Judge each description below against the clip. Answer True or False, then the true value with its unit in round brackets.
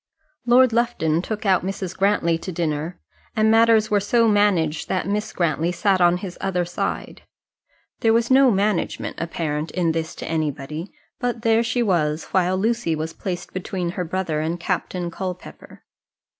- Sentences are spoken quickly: False (160 wpm)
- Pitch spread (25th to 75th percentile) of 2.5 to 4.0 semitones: False (4.5 semitones)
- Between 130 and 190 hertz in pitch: True (185 Hz)